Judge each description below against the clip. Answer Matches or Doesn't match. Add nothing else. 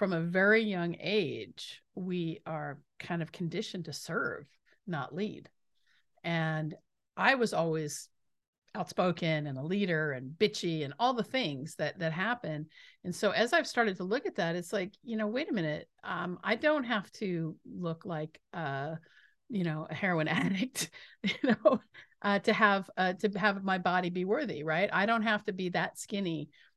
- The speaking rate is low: Doesn't match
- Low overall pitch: Doesn't match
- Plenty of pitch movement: Doesn't match